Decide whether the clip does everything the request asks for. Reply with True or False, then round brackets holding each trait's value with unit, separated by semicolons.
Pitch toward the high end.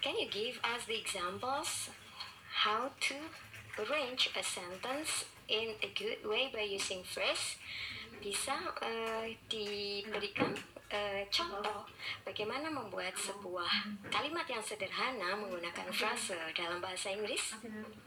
True (210 Hz)